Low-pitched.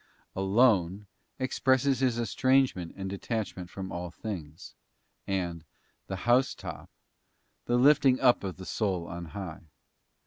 Yes: low, 100 Hz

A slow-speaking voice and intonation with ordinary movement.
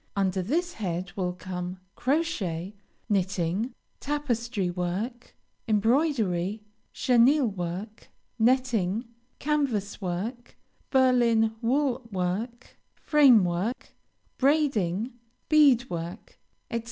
No: slow, 85 wpm; wide, 5.9 semitones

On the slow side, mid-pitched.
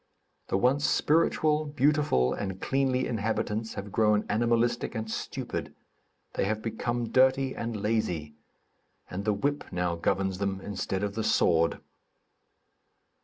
No: slow, 125 wpm; low, 110 Hz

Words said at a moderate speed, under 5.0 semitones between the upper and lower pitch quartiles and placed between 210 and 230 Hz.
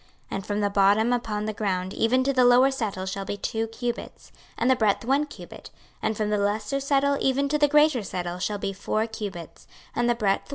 No: fast, 235 wpm; average, 4.2 semitones; high, 220 Hz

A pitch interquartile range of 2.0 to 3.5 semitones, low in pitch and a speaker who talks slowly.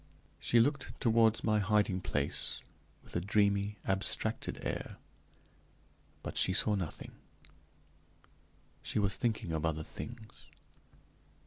Yes: average, 3.0 semitones; low, 100 Hz; slow, 110 wpm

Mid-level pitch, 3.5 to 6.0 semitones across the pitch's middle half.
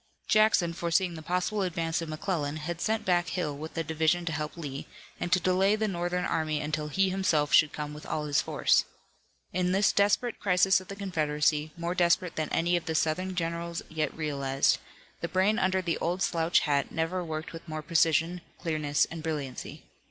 No: medium, 165 Hz; average, 2.9 semitones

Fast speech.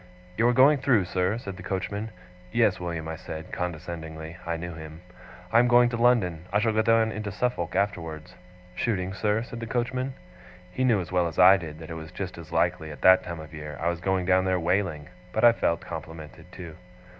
Yes: fast, 215 wpm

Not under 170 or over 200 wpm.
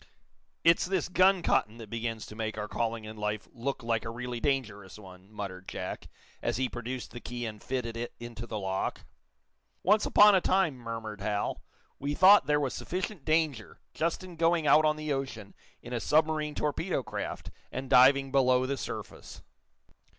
Yes: average, 180 wpm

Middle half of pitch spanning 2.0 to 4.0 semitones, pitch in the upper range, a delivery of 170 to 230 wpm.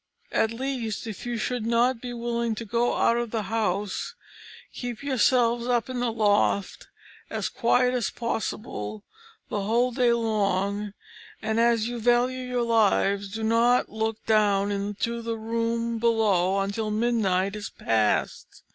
No: narrow, 2.4 semitones; high, 230 Hz; average, 145 wpm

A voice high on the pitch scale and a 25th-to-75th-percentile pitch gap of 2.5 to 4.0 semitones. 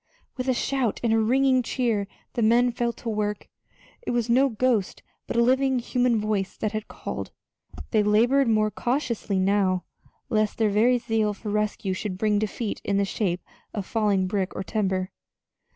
Yes: high, 215 Hz; average, 2.9 semitones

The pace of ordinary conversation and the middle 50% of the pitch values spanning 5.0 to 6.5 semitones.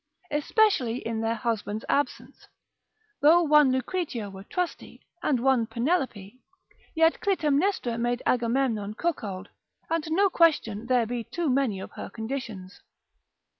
No: slow, 125 wpm; wide, 5.5 semitones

